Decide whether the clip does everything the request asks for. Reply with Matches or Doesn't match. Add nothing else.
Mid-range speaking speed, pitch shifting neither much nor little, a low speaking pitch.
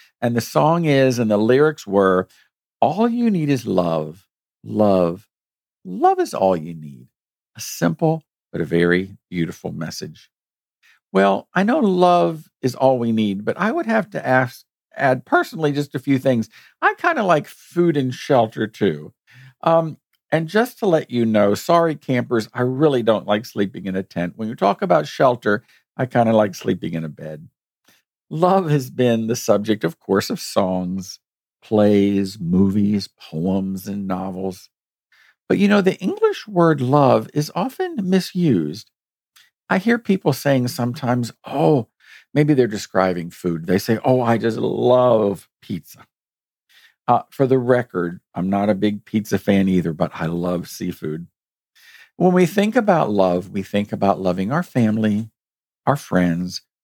Doesn't match